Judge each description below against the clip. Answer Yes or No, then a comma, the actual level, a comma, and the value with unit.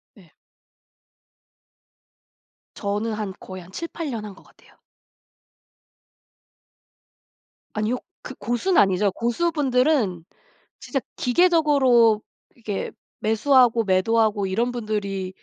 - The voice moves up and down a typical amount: Yes, average, 4.1 semitones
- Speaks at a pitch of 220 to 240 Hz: Yes, high, 225 Hz